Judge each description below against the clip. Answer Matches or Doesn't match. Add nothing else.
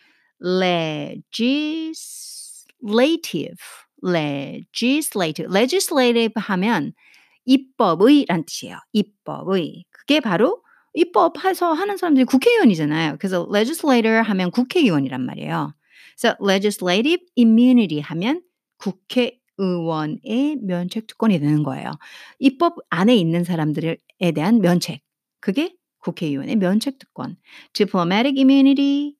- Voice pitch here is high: Matches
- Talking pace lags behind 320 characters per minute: Doesn't match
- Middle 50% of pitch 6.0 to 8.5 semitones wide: Matches